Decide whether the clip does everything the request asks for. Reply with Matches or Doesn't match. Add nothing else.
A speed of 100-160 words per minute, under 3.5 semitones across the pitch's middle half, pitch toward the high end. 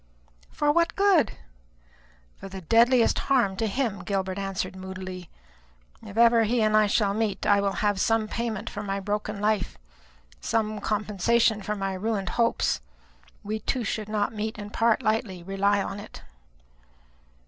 Matches